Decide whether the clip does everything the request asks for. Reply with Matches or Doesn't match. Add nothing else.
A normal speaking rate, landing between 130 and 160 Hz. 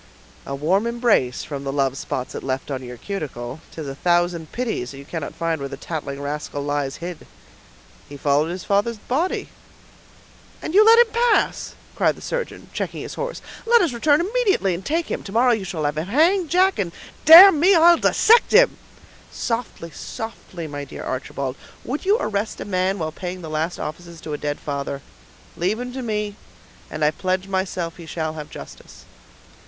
Doesn't match